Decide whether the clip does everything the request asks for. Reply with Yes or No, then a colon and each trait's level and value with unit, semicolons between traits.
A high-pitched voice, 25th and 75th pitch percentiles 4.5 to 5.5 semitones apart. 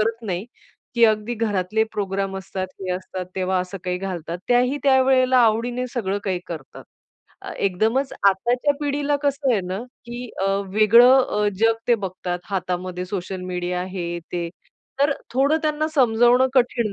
Yes: high, 215 Hz; average, 5.1 semitones